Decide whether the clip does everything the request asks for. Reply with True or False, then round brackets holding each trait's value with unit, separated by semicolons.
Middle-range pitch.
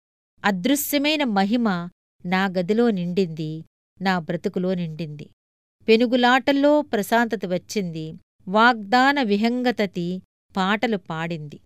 False (205 Hz)